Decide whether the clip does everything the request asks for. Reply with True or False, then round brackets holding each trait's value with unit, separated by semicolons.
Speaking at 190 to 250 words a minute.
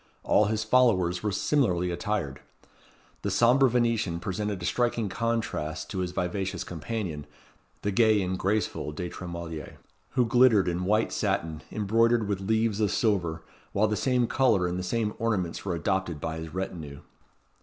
False (155 wpm)